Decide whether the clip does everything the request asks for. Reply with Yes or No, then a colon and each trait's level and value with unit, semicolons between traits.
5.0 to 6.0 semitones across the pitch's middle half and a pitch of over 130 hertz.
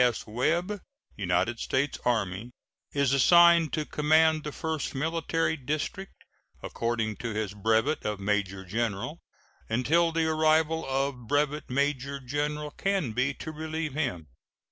Yes: average, 5.3 semitones; medium, 140 Hz